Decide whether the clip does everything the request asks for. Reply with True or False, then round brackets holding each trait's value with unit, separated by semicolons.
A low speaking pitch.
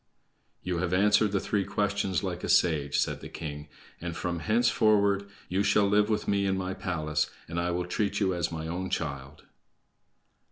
True (90 Hz)